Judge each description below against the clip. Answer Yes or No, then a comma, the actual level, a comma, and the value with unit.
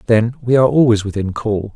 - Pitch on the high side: No, low, 110 Hz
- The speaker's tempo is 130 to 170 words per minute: No, fast, 205 wpm